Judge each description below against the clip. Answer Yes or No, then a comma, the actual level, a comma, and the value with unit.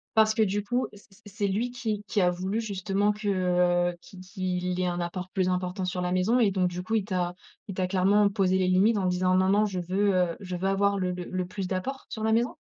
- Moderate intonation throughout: No, narrow, 2.3 semitones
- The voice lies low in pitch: No, high, 190 Hz